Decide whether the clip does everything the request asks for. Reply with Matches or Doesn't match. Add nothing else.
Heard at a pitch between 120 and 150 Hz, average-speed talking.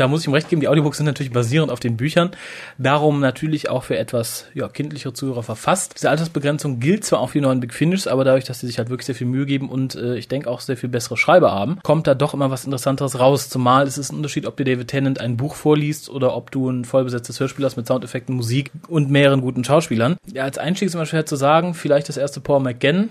Doesn't match